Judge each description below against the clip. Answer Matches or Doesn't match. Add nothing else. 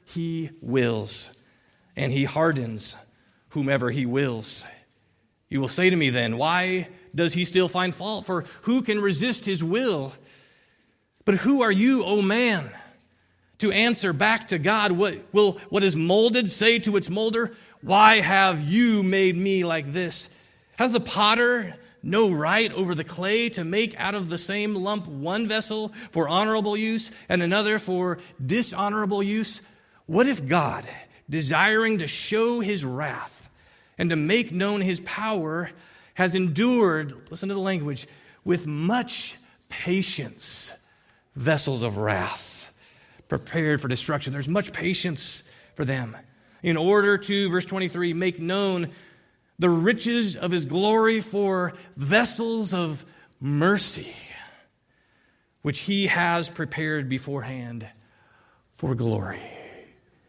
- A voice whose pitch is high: Doesn't match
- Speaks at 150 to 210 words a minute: Doesn't match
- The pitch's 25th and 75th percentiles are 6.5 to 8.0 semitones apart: Doesn't match